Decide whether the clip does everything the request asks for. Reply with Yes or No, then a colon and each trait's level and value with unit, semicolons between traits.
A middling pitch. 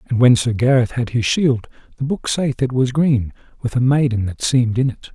No: low, 125 Hz